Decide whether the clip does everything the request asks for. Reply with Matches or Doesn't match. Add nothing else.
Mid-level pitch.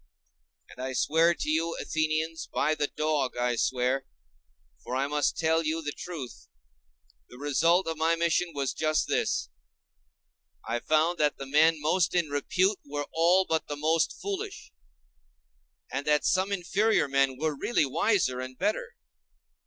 Matches